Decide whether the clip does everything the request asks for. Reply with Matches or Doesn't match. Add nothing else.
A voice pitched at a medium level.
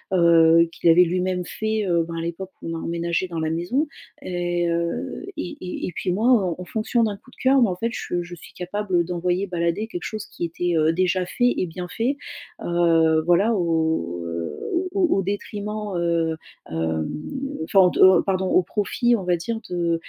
Matches